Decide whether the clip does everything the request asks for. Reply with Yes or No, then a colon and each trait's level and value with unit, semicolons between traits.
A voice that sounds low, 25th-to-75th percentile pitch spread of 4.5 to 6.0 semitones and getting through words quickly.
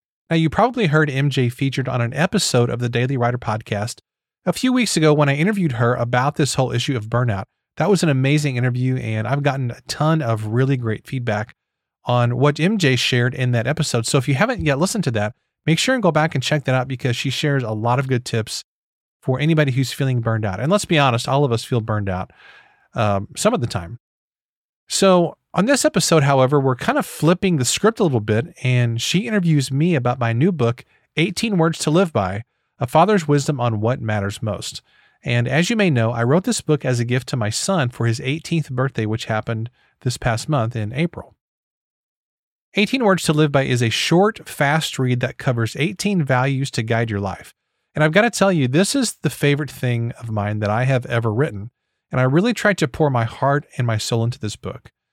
Yes: low, 130 Hz; average, 5.0 semitones; fast, 225 wpm